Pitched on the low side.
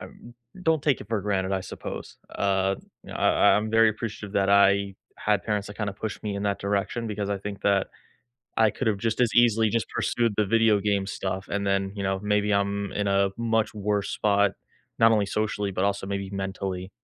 Yes: low, 100 Hz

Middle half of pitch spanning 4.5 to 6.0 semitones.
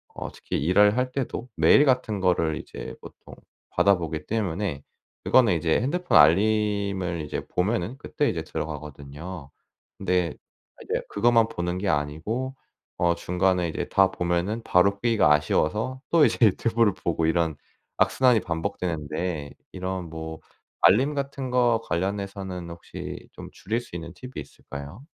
Yes: average, 5.3 semitones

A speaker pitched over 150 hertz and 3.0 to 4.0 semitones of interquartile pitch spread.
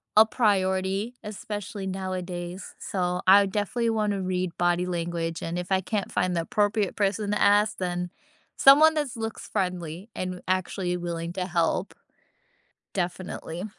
No: medium, 185 Hz; narrow, 2.6 semitones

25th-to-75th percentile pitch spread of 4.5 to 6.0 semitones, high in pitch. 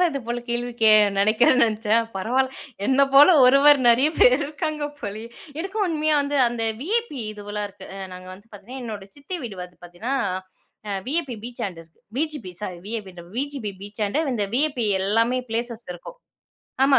Yes: average, 5.3 semitones; high, 240 Hz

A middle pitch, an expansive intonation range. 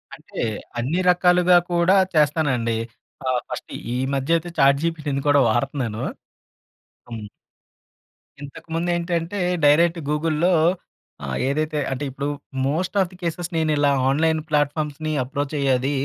No: medium, 150 Hz; average, 3.5 semitones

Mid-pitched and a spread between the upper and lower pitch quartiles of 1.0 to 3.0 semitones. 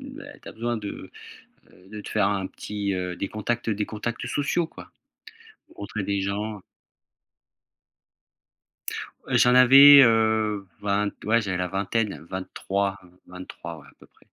No: low, 105 Hz; narrow, 2.6 semitones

